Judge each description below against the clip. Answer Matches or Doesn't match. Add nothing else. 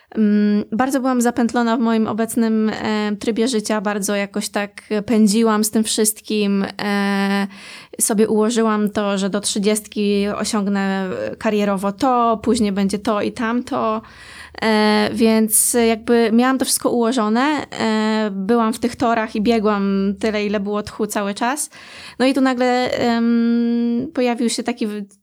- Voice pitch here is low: Doesn't match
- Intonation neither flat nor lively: Doesn't match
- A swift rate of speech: Doesn't match